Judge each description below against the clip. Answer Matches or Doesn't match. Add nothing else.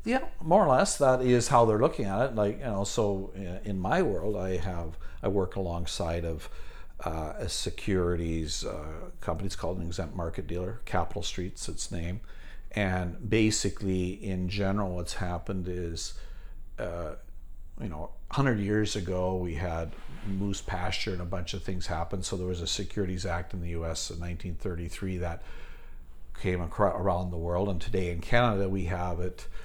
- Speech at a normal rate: Matches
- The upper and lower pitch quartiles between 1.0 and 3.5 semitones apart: Matches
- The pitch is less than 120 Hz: Matches